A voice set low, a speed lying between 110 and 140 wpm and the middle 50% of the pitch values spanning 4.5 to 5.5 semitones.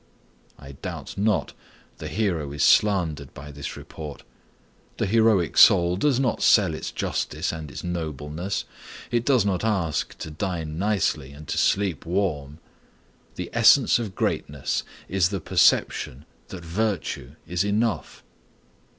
Yes: very low, 90 Hz; slow, 135 wpm; average, 5.1 semitones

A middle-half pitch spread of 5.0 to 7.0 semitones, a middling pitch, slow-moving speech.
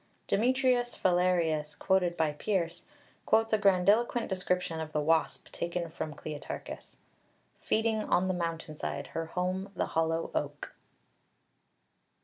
No: average, 3.6 semitones; medium, 180 Hz; slow, 120 wpm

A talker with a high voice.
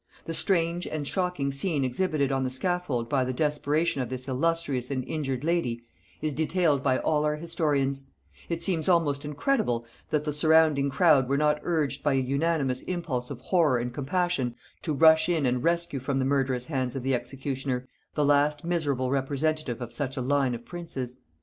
No: medium, 145 Hz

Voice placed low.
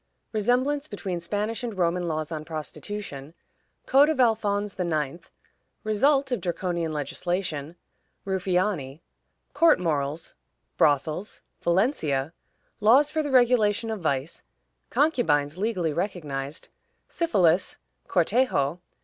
No: medium, 185 Hz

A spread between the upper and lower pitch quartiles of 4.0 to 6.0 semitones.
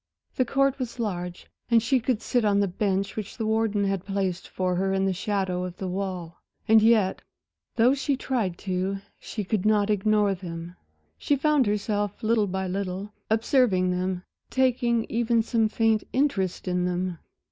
No: average, 3.5 semitones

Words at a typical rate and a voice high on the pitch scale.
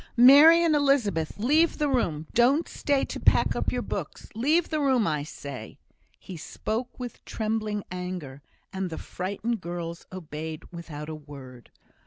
Yes: average, 155 wpm; high, 200 Hz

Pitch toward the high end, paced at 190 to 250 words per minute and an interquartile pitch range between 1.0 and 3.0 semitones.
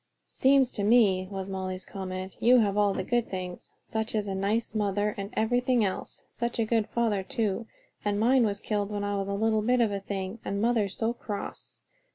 Yes: high, 205 Hz; average, 200 wpm; average, 2.7 semitones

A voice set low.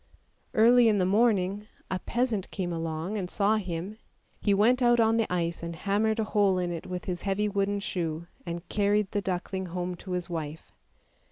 No: high, 195 Hz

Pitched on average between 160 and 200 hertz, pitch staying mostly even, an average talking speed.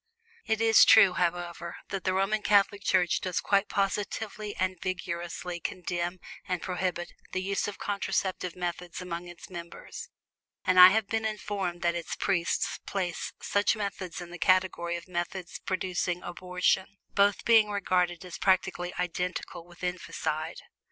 Yes: medium, 185 Hz; narrow, 2.1 semitones; average, 145 wpm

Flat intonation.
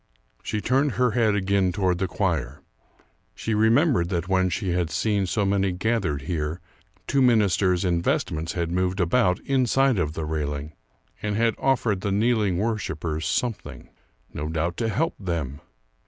No: average, 4.7 semitones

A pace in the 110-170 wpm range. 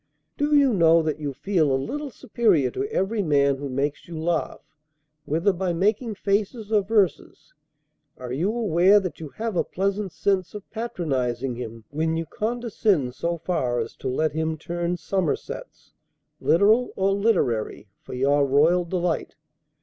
Yes: average, 155 wpm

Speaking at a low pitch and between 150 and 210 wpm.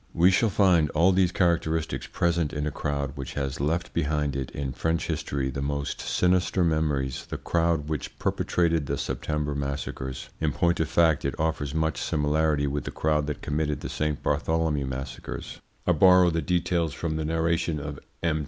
Yes: very low, 80 Hz; average, 180 wpm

